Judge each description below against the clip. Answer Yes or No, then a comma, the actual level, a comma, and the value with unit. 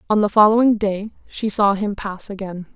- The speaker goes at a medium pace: Yes, average, 195 wpm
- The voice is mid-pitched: No, high, 205 Hz